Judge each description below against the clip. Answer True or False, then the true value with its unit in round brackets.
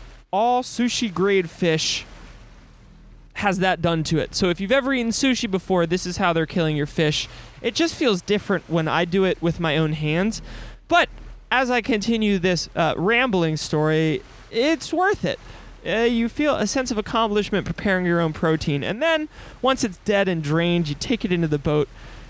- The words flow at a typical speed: True (190 wpm)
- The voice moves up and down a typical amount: False (6.2 semitones)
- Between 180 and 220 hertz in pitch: True (185 Hz)